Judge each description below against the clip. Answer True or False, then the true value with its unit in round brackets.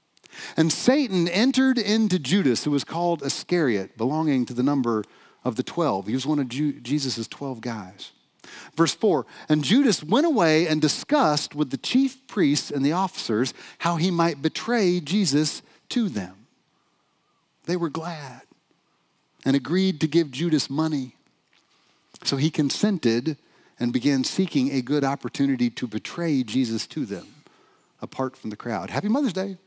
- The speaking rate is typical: True (150 wpm)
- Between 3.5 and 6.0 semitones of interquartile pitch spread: True (5.2 semitones)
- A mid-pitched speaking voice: True (155 Hz)